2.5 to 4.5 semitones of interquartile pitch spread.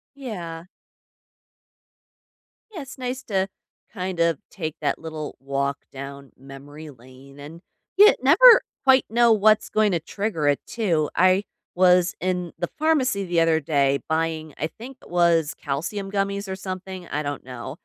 No: wide, 5.5 semitones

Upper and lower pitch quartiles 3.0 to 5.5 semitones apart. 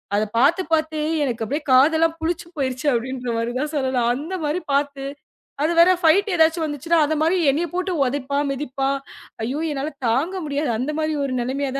Yes: average, 3.5 semitones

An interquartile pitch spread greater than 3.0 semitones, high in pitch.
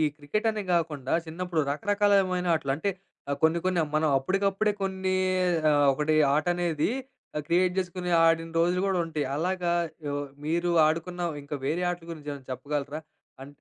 No: average, 3.5 semitones; medium, 165 Hz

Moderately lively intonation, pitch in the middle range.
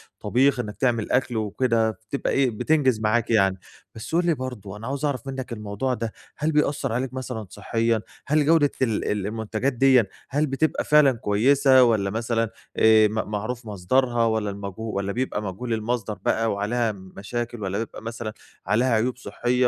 No: average, 3.3 semitones; low, 115 Hz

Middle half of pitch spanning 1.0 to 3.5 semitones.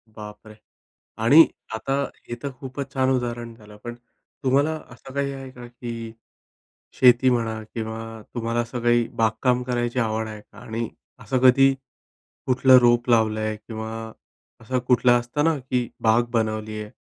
Yes: narrow, 2.5 semitones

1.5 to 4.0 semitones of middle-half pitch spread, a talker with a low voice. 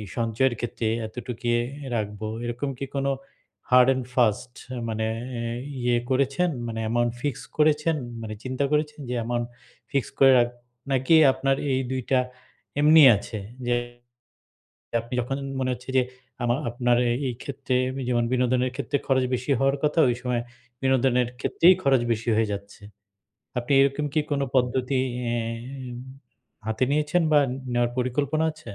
Yes: narrow, 2.4 semitones; low, 125 Hz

